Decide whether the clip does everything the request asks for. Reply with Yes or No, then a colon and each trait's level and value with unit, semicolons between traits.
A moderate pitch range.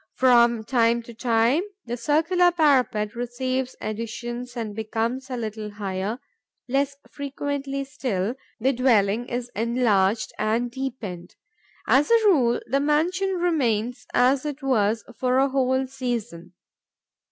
Yes: average, 3.3 semitones